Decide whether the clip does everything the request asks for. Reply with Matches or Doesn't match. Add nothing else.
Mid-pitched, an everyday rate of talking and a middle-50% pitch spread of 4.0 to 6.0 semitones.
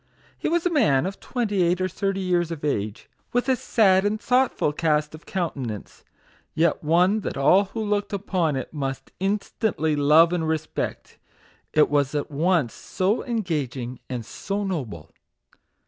Matches